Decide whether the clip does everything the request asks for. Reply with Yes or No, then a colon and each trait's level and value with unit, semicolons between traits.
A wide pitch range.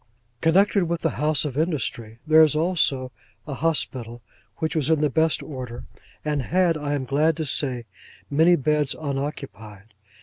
No: average, 3.5 semitones